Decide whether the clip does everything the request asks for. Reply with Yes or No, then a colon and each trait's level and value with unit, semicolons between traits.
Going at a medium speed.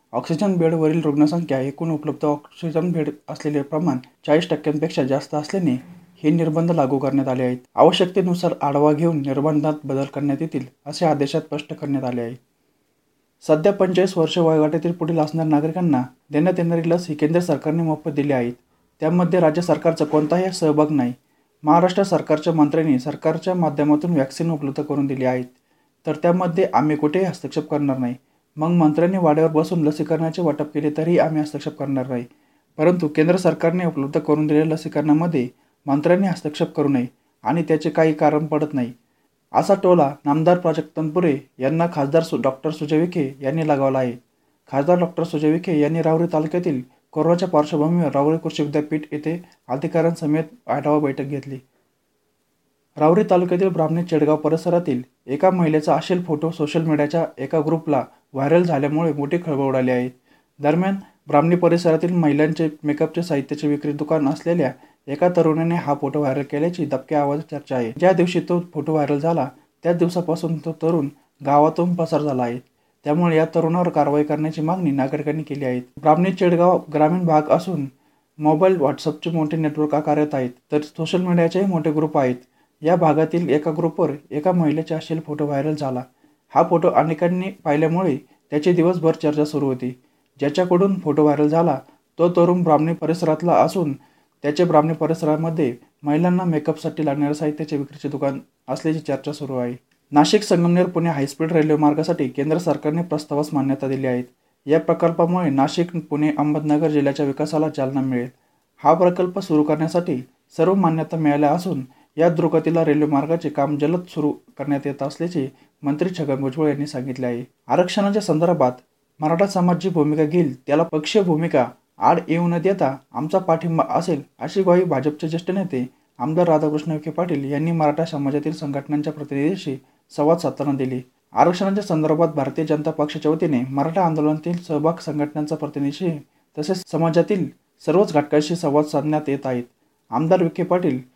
No: fast, 145 wpm